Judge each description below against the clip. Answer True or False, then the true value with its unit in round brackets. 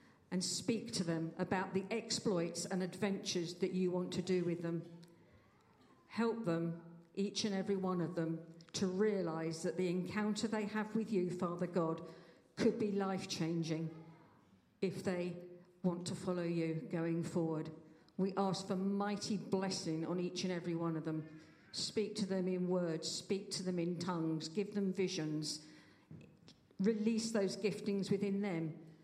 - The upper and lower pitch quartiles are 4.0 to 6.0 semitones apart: False (2.9 semitones)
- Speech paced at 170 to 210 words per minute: False (160 wpm)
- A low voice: False (180 Hz)